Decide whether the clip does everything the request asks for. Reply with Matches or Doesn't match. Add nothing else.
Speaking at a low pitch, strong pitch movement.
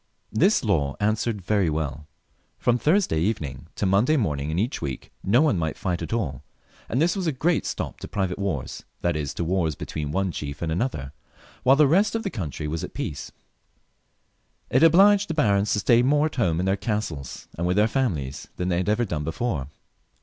Matches